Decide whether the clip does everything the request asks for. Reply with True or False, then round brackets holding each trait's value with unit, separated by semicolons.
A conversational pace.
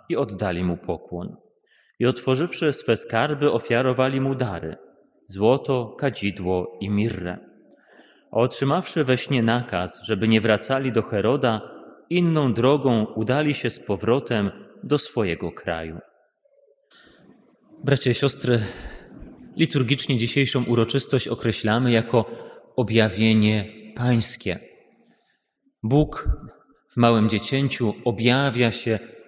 False (100 wpm)